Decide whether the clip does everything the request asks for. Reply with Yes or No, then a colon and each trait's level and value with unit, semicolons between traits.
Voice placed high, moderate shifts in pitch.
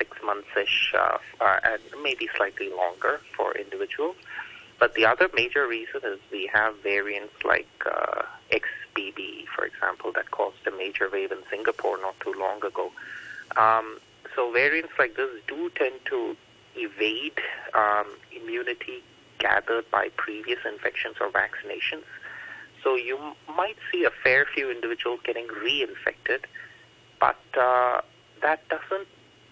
Yes: very high, 390 Hz; average, 4.1 semitones